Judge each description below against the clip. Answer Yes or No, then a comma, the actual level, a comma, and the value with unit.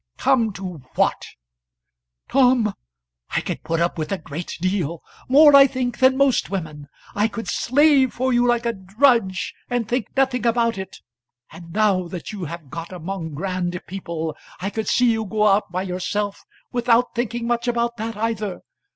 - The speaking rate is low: No, average, 170 wpm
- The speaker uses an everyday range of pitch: Yes, average, 5.0 semitones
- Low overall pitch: No, high, 210 Hz